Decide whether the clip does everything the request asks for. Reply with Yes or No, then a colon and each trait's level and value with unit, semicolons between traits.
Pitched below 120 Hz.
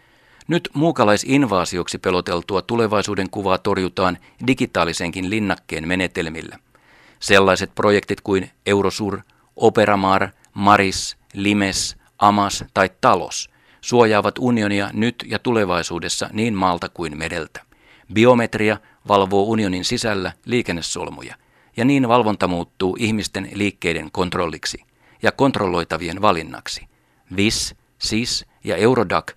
Yes: low, 100 Hz